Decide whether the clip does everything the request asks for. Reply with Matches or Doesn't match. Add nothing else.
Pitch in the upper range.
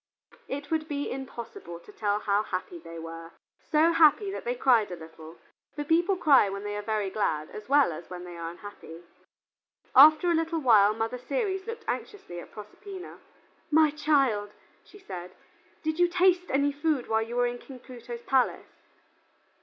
Matches